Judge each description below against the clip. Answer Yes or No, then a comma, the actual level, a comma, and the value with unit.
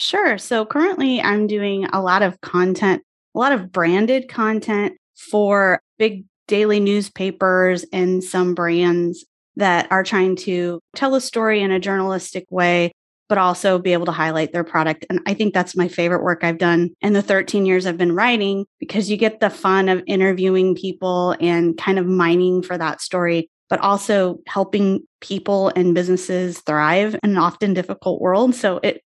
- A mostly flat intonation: Yes, narrow, 2.3 semitones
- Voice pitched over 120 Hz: Yes, high, 190 Hz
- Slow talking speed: No, average, 175 wpm